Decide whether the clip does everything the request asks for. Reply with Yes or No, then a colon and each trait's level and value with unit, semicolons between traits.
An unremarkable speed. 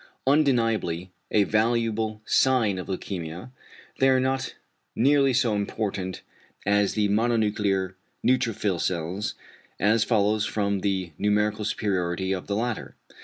No: slow, 120 wpm